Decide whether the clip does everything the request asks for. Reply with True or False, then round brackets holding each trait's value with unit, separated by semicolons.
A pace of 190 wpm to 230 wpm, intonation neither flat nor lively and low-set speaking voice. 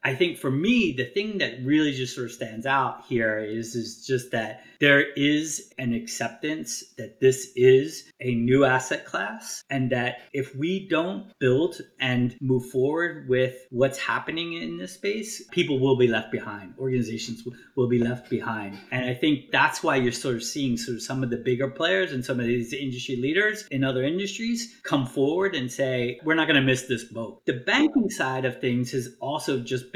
True (195 wpm; 3.0 semitones; 130 Hz)